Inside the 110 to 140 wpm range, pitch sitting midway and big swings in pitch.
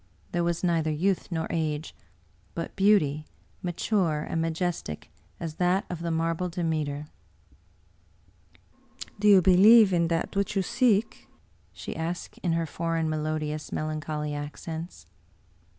No: slow, 135 wpm; medium, 165 Hz; average, 2.7 semitones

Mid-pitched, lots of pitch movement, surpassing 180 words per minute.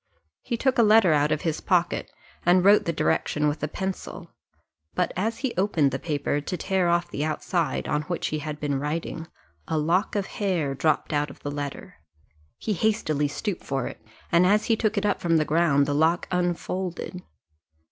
No: medium, 170 Hz; average, 4.3 semitones; average, 195 wpm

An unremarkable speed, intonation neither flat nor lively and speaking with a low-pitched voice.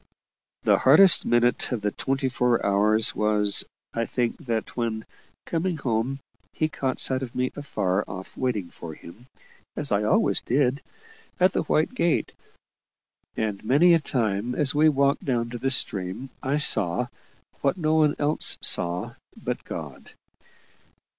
Yes: average, 150 wpm; average, 4.9 semitones; low, 125 Hz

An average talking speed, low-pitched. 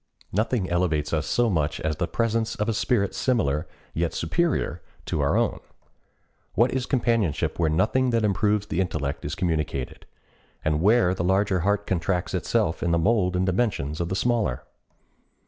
Yes: average, 165 wpm; very low, 95 Hz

